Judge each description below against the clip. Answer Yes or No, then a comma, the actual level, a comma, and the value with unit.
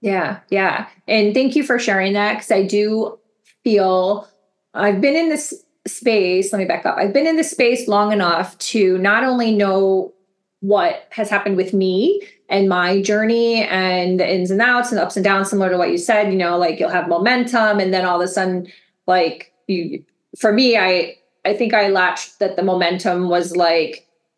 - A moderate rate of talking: Yes, average, 195 wpm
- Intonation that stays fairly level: No, average, 3.3 semitones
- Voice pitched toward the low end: No, high, 200 Hz